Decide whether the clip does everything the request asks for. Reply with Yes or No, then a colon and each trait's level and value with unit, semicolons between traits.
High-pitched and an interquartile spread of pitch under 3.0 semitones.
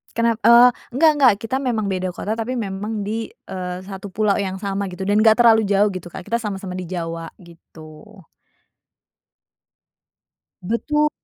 No: high, 205 Hz; average, 3.7 semitones